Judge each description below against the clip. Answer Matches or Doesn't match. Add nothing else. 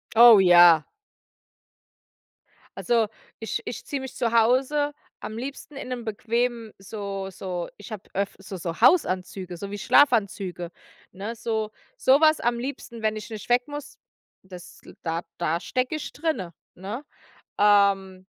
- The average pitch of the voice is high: Matches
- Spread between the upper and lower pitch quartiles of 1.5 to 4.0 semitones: Doesn't match